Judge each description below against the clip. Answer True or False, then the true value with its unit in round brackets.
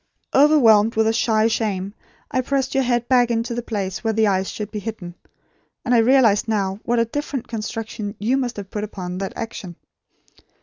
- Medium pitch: False (225 Hz)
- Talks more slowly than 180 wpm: False (190 wpm)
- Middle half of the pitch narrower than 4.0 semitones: True (2.8 semitones)